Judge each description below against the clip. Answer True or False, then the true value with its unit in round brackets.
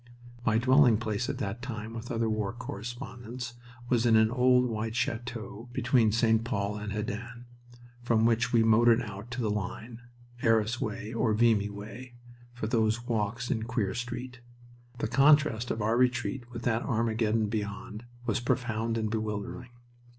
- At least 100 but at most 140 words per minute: False (160 wpm)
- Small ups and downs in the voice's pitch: True (1.9 semitones)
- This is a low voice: True (115 Hz)